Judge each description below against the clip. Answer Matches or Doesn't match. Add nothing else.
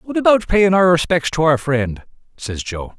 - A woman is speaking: Doesn't match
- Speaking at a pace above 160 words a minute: Matches